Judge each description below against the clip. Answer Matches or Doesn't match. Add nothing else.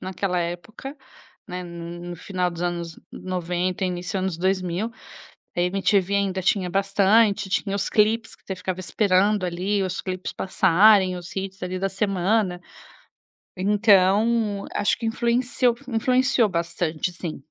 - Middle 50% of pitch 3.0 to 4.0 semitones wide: Doesn't match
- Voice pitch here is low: Doesn't match